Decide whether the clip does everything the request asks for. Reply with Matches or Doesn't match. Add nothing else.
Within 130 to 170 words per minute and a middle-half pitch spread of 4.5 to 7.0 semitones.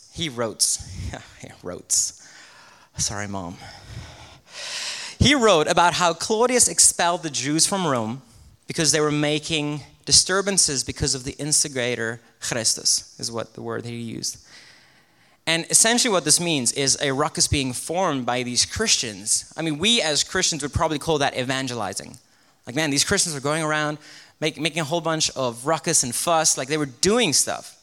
Matches